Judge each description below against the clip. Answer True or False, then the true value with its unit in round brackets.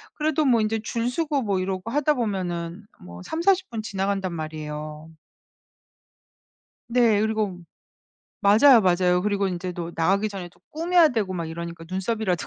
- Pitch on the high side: True (200 Hz)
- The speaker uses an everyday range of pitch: True (4.8 semitones)